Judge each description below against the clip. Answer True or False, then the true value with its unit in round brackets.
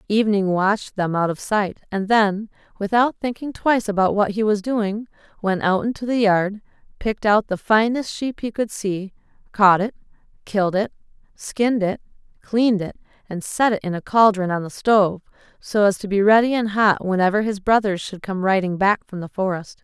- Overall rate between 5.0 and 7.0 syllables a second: True (5.2 syllables/s)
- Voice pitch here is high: True (205 Hz)